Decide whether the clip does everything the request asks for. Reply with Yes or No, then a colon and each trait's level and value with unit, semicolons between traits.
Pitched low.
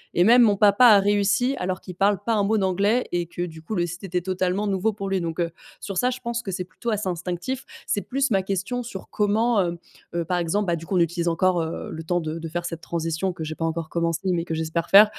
No: medium, 185 Hz